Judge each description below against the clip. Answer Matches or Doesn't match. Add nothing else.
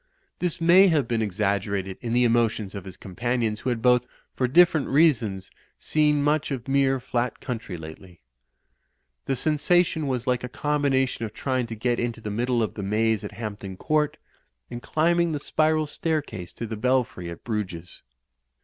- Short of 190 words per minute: Matches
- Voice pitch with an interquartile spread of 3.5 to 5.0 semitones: Doesn't match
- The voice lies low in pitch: Matches